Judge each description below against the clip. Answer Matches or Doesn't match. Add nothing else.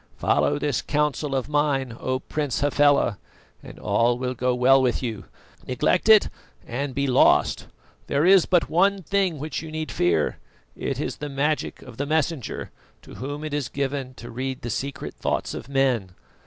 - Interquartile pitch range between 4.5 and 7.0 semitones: Doesn't match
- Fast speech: Doesn't match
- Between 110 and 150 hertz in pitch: Matches